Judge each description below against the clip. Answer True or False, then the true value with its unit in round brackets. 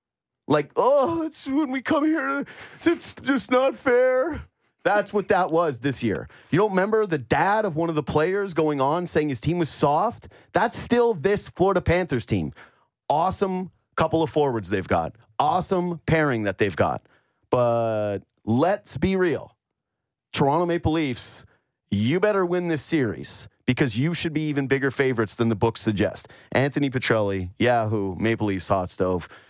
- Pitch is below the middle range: False (155 Hz)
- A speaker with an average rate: True (165 wpm)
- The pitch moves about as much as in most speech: False (8.6 semitones)